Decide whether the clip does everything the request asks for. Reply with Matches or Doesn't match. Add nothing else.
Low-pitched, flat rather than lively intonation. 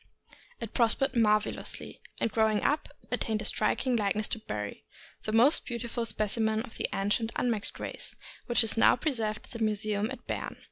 Doesn't match